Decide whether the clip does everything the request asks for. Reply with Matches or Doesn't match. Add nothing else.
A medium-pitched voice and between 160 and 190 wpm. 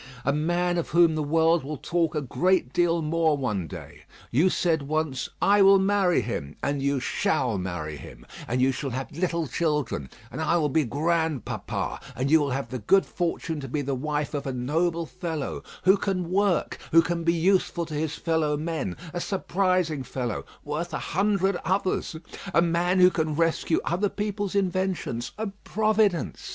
Matches